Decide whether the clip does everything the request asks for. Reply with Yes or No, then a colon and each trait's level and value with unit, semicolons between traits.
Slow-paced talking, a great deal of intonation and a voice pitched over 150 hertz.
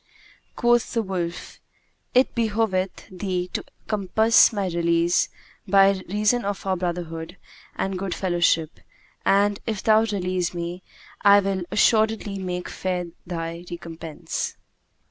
No: slow, 120 wpm; average, 3.0 semitones; high, 190 Hz